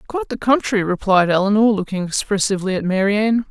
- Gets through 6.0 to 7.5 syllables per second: Yes, 6.6 syllables/s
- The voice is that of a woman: Yes, female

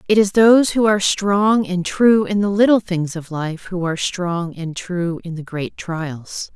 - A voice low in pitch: No, medium, 185 Hz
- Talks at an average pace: No, fast, 210 wpm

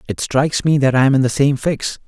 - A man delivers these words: Yes, male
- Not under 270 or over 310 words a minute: Yes, fast, 290 wpm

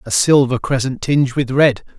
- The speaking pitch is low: Yes, low, 130 Hz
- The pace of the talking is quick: No, average, 180 wpm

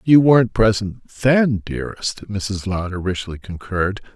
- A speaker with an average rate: No, slow, 130 wpm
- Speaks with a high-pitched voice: No, low, 105 Hz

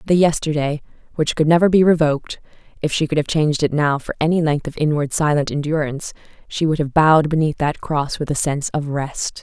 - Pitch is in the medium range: Yes, medium, 150 Hz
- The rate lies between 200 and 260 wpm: Yes, fast, 205 wpm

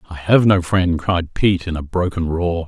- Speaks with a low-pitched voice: Yes, very low, 85 Hz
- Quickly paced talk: Yes, fast, 225 wpm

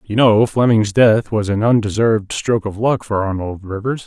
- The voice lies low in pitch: Yes, low, 110 Hz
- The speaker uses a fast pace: No, average, 190 wpm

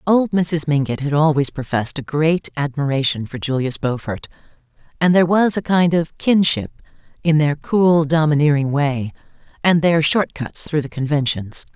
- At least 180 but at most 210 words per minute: No, average, 160 wpm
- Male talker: No, female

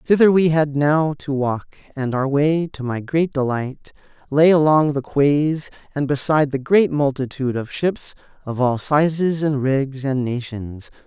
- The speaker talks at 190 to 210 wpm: No, average, 170 wpm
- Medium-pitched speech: Yes, medium, 145 Hz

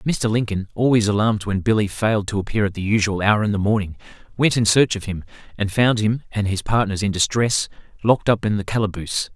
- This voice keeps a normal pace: No, fast, 220 wpm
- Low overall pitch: Yes, low, 105 Hz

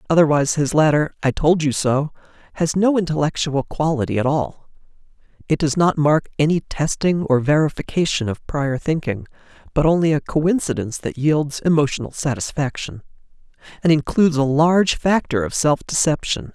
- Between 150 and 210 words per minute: No, average, 140 wpm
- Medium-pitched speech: Yes, medium, 150 Hz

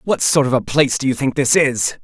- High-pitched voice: No, low, 135 Hz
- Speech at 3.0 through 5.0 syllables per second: No, 5.9 syllables/s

